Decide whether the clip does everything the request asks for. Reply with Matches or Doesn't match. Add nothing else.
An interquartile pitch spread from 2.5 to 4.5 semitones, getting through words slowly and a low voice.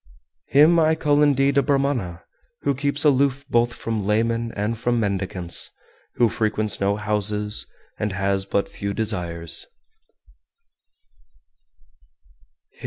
Doesn't match